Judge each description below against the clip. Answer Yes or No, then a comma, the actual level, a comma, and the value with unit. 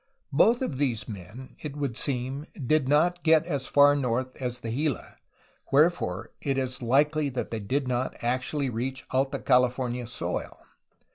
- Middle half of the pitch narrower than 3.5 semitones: Yes, average, 2.8 semitones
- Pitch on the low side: Yes, low, 130 Hz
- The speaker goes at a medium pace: Yes, average, 155 wpm